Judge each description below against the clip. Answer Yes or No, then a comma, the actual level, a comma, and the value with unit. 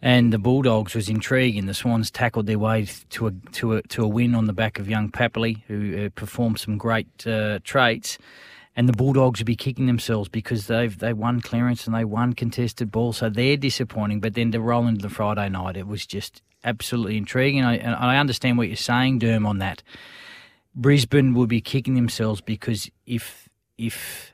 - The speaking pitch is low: Yes, low, 115 Hz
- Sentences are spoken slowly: No, average, 200 wpm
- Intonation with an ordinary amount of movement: No, narrow, 2.1 semitones